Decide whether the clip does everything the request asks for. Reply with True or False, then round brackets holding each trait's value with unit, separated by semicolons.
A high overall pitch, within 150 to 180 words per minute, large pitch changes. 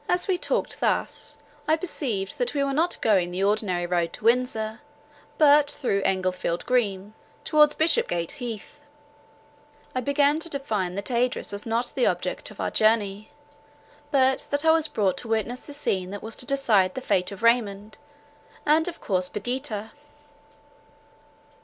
True (230 Hz; 155 wpm; 6.3 semitones)